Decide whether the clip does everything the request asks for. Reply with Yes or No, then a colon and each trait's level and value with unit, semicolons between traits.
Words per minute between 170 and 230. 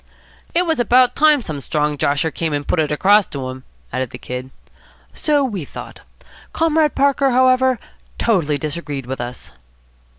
No: average, 160 wpm